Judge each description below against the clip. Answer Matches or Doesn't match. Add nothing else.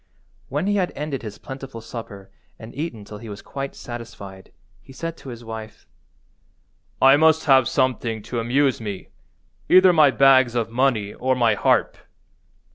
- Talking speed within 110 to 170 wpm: Matches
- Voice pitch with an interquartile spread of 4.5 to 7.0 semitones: Doesn't match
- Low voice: Matches